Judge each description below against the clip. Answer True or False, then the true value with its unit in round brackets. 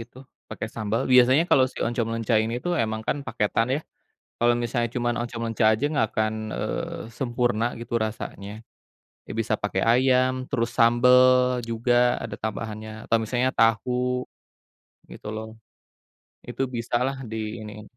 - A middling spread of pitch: False (2.1 semitones)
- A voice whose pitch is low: True (115 Hz)